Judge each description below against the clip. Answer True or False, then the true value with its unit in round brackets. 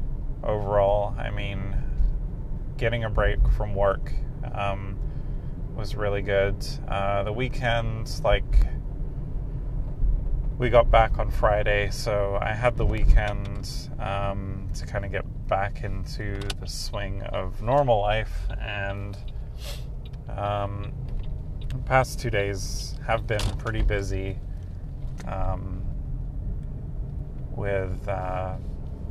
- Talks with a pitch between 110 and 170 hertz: False (100 Hz)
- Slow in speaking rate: True (105 wpm)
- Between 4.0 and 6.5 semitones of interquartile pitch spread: False (2.6 semitones)